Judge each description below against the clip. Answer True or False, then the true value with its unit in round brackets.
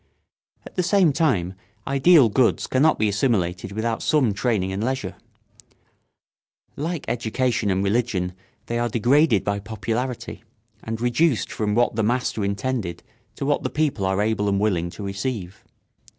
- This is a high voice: False (115 Hz)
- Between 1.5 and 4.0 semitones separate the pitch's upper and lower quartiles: False (4.5 semitones)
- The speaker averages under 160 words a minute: True (150 wpm)